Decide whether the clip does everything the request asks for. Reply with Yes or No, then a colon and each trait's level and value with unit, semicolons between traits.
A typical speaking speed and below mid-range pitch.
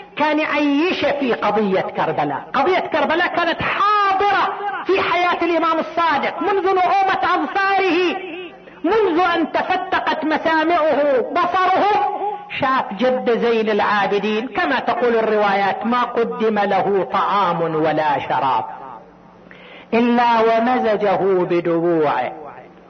No: average, 95 wpm; very high, 295 Hz